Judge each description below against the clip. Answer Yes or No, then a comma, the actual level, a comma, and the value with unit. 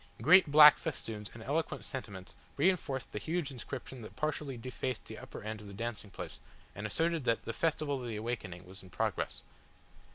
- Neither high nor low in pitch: No, low, 125 Hz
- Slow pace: No, average, 185 wpm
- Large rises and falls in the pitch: Yes, wide, 6.0 semitones